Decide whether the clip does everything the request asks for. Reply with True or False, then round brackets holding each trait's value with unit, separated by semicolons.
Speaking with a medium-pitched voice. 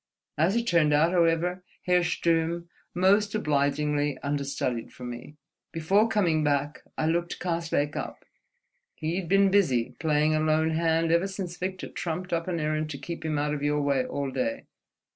True (160 Hz)